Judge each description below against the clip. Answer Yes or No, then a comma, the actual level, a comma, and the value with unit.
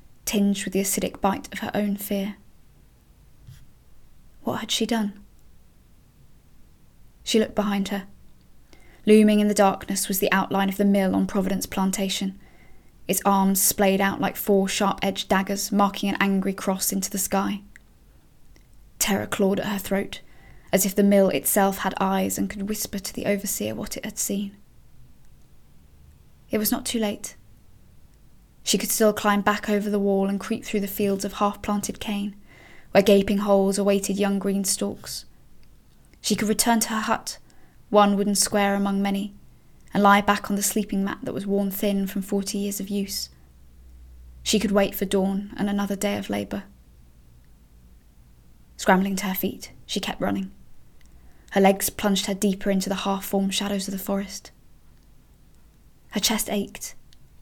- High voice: Yes, high, 200 Hz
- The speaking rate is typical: Yes, average, 165 wpm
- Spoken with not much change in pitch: Yes, narrow, 1.1 semitones